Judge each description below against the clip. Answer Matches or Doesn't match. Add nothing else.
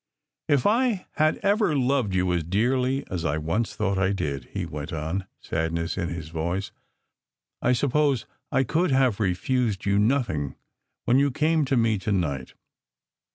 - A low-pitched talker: Matches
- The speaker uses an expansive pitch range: Matches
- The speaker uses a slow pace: Doesn't match